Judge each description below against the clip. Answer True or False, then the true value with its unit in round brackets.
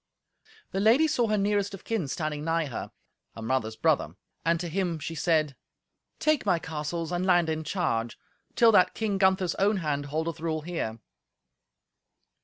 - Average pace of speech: True (155 wpm)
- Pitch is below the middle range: False (170 Hz)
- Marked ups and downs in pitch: False (4.2 semitones)